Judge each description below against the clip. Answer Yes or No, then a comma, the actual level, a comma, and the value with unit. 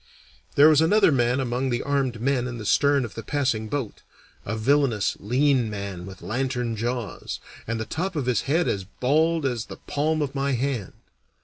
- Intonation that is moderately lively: Yes, average, 3.9 semitones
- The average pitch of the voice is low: Yes, low, 130 Hz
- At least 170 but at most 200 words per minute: Yes, average, 190 wpm